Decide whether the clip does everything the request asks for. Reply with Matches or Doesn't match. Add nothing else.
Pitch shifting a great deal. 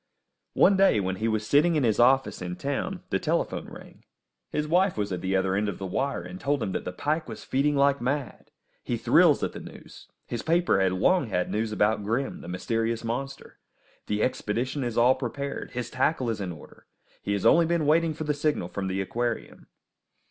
Matches